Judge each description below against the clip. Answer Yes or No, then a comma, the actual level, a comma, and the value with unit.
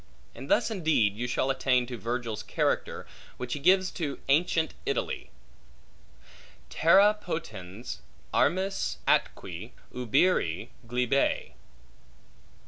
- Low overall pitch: Yes, low, 130 Hz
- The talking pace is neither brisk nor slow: No, slow, 100 wpm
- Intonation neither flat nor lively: No, wide, 6.5 semitones